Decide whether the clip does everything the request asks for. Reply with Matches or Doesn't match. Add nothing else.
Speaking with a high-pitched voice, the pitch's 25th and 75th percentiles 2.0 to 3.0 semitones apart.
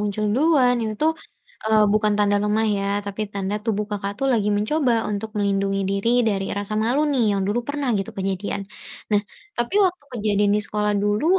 Matches